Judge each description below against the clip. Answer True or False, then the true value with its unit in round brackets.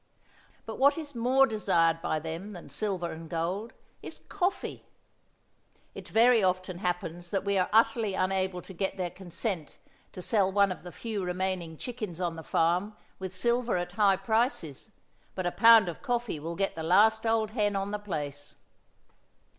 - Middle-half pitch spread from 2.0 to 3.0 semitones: False (4.0 semitones)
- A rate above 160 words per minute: True (170 wpm)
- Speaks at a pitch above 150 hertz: True (190 Hz)